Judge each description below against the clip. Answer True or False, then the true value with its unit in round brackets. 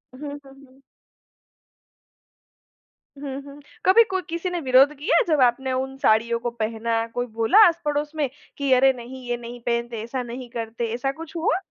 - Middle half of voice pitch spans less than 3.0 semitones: False (3.6 semitones)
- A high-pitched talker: True (260 Hz)